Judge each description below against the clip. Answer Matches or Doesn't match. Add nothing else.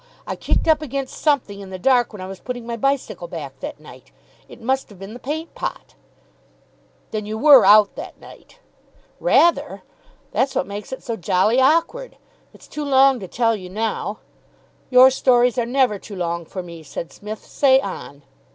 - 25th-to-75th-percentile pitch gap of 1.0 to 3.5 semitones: Doesn't match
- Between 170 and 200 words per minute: Matches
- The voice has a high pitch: Matches